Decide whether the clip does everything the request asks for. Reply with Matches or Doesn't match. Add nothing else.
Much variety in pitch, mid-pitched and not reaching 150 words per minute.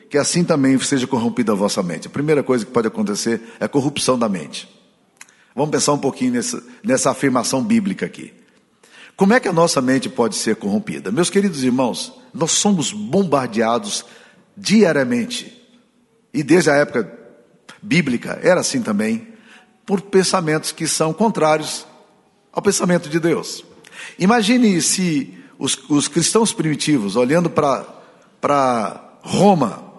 Matches